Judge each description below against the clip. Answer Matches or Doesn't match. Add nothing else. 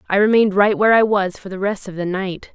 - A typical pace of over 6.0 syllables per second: Matches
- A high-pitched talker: Matches